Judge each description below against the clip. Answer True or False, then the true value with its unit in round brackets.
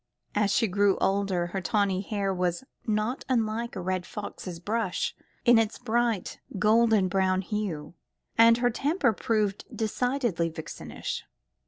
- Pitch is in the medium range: False (210 Hz)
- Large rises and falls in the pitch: False (3.5 semitones)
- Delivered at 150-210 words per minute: False (135 wpm)